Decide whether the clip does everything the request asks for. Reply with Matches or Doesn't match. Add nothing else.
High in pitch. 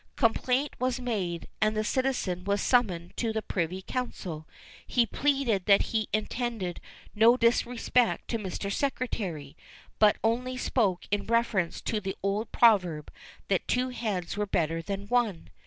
Matches